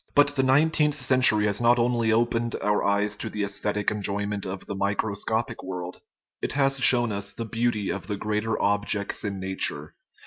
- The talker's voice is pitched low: Yes, low, 105 Hz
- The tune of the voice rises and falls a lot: No, average, 3.0 semitones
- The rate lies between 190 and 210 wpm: No, average, 175 wpm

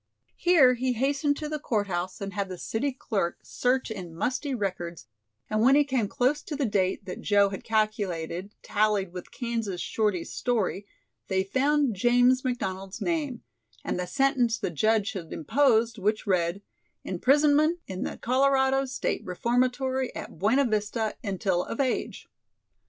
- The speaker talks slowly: No, average, 155 wpm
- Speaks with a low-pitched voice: No, high, 225 Hz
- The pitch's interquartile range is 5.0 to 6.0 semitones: Yes, wide, 5.4 semitones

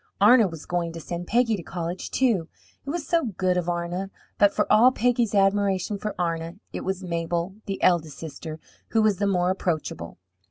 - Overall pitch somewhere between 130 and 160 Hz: No, medium, 185 Hz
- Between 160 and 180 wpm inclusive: No, average, 190 wpm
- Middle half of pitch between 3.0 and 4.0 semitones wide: Yes, average, 3.5 semitones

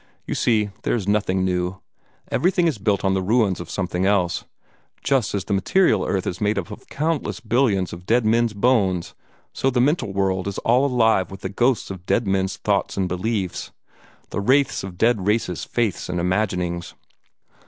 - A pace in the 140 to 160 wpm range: No, average, 185 wpm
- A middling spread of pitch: Yes, average, 4.2 semitones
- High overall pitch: No, low, 100 Hz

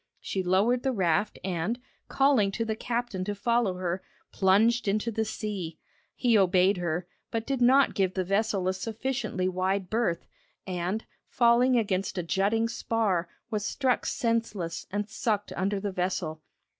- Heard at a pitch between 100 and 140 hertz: No, high, 205 Hz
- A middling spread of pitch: Yes, average, 3.7 semitones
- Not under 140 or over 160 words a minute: Yes, average, 155 wpm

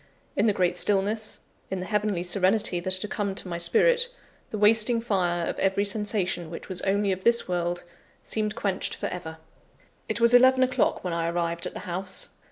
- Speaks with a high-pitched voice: Yes, high, 195 Hz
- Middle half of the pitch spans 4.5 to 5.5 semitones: No, average, 3.3 semitones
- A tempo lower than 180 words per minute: No, average, 190 wpm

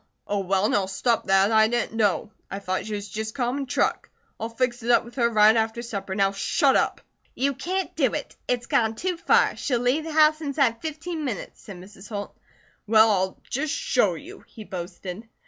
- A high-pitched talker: Yes, high, 225 Hz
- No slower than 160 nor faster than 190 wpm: No, average, 200 wpm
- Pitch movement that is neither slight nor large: Yes, average, 4.5 semitones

